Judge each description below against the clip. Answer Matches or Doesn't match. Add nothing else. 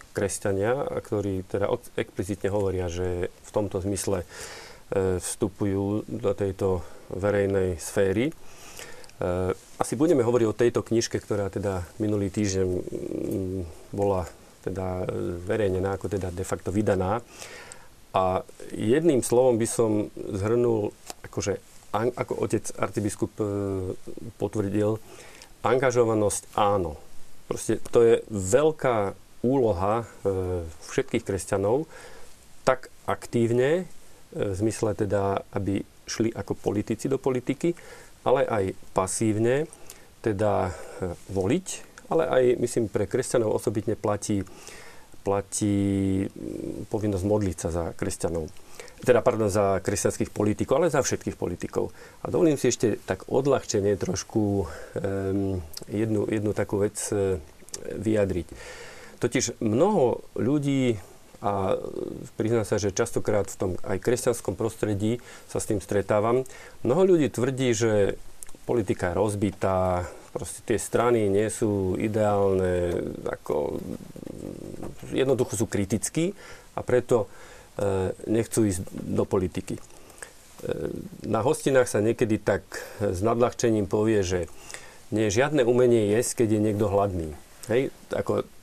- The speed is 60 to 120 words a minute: Matches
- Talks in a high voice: Doesn't match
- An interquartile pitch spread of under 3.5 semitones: Matches